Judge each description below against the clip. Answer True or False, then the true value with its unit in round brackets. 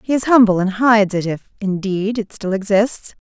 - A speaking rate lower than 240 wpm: True (205 wpm)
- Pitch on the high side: True (205 Hz)